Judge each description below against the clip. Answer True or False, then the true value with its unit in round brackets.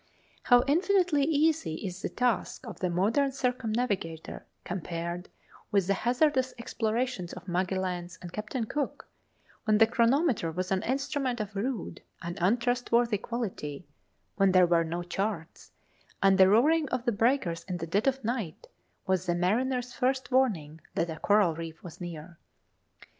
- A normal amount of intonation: False (6.1 semitones)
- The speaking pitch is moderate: False (210 Hz)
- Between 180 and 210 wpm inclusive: False (150 wpm)